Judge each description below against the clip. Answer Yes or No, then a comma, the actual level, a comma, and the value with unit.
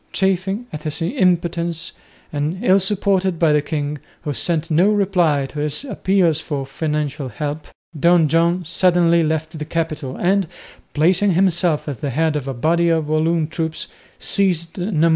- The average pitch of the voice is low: No, medium, 165 Hz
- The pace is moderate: Yes, average, 160 wpm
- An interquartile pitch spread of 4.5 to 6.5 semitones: No, average, 3.0 semitones